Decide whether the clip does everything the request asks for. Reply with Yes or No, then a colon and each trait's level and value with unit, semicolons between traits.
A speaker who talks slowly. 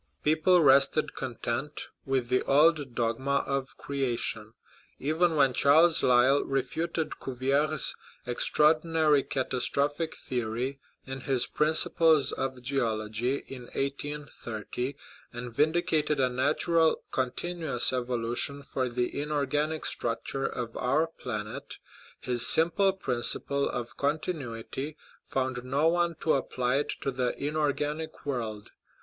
Yes: slow, 115 wpm